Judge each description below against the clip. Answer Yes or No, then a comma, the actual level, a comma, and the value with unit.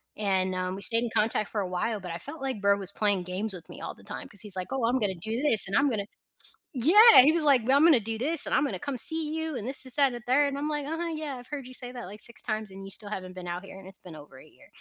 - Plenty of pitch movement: Yes, wide, 6.3 semitones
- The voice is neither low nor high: No, high, 225 Hz